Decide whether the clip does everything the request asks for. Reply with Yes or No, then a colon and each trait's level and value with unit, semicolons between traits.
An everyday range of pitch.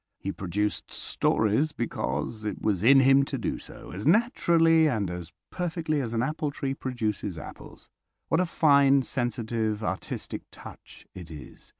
No: wide, 6.2 semitones